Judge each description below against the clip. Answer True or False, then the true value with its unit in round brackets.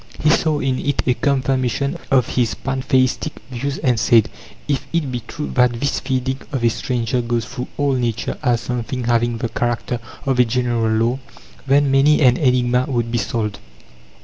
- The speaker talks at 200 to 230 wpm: False (175 wpm)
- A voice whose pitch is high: False (125 Hz)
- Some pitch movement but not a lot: False (2.3 semitones)